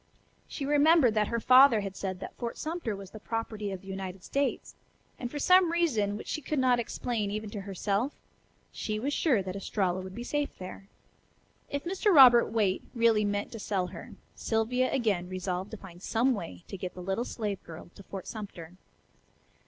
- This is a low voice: No, high, 215 Hz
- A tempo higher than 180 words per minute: Yes, average, 190 wpm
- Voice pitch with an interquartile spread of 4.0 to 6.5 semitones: Yes, average, 4.7 semitones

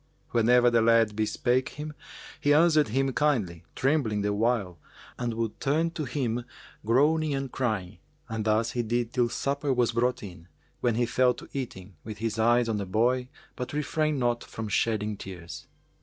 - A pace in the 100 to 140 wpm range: No, average, 170 wpm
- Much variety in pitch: No, average, 3.6 semitones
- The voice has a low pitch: Yes, low, 120 Hz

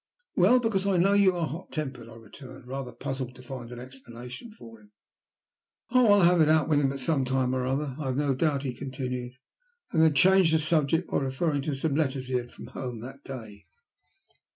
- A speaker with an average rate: No, fast, 220 wpm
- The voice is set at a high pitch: No, low, 135 Hz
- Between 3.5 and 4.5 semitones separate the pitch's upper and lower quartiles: Yes, average, 4.0 semitones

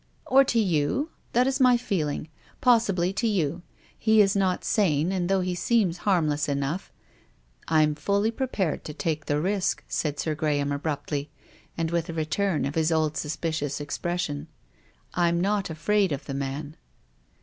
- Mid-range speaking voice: Yes, medium, 165 Hz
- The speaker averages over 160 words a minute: Yes, average, 180 wpm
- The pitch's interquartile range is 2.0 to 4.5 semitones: No, average, 5.0 semitones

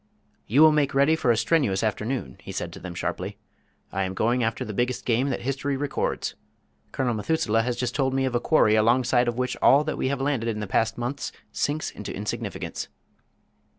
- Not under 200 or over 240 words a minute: Yes, fast, 205 wpm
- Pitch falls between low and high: No, low, 125 Hz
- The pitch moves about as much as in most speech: Yes, average, 3.6 semitones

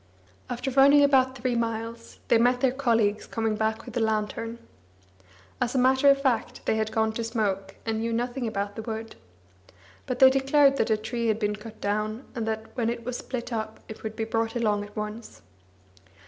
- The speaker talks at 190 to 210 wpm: Yes, average, 200 wpm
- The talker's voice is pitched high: Yes, high, 230 Hz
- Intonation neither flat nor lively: No, narrow, 2.2 semitones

